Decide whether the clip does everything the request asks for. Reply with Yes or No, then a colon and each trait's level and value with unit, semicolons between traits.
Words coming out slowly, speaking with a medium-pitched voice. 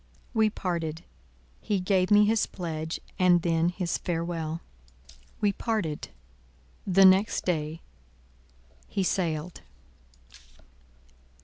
Yes: slow, 90 wpm; medium, 175 Hz